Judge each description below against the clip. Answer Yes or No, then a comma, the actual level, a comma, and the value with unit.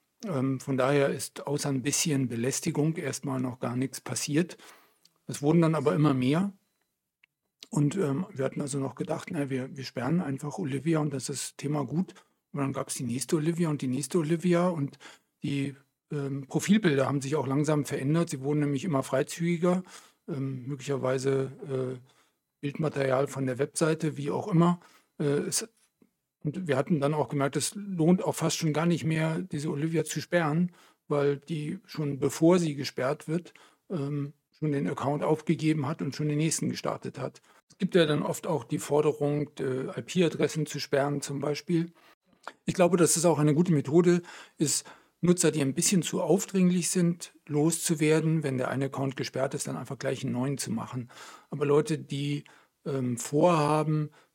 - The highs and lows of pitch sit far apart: No, average, 3.3 semitones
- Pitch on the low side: No, medium, 150 Hz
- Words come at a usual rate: Yes, average, 175 wpm